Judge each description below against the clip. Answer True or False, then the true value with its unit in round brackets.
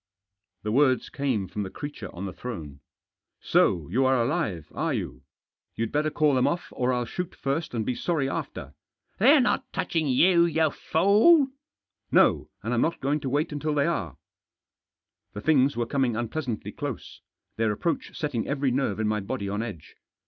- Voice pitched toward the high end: False (130 Hz)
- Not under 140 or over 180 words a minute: False (190 wpm)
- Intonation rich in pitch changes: True (5.8 semitones)